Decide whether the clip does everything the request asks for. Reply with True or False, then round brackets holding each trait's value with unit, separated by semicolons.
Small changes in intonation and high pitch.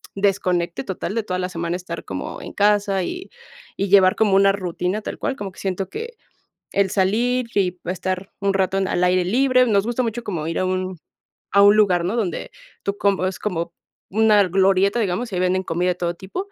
True (2.3 semitones; 195 Hz)